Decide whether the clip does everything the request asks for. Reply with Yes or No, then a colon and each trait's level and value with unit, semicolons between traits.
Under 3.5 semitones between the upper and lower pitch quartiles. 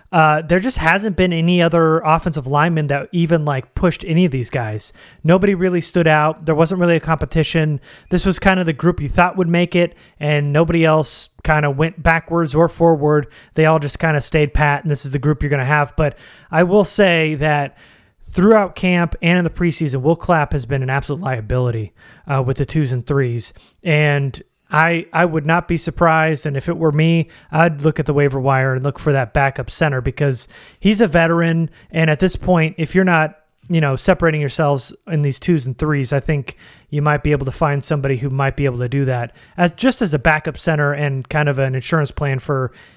Yes: average, 2.9 semitones